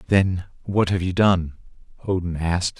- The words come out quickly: No, average, 150 wpm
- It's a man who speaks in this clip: Yes, male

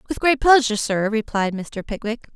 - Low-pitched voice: No, high, 230 Hz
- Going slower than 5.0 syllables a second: No, 5.4 syllables/s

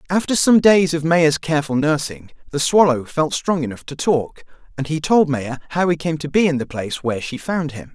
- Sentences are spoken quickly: Yes, fast, 225 wpm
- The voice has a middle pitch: Yes, medium, 155 Hz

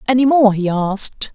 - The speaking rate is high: No, average, 180 wpm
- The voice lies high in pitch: Yes, high, 225 Hz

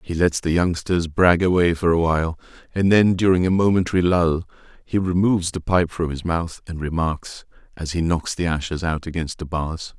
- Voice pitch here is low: Yes, very low, 85 Hz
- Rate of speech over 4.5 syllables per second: Yes, 5.1 syllables/s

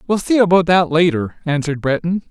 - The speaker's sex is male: Yes, male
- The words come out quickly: No, average, 180 wpm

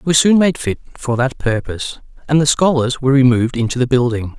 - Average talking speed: No, fast, 220 wpm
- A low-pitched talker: Yes, low, 130 Hz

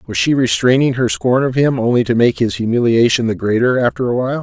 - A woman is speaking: No, male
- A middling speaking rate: No, fast, 230 wpm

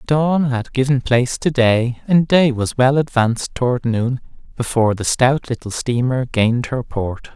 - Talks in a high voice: No, low, 125 Hz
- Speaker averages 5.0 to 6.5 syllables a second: No, 4.5 syllables/s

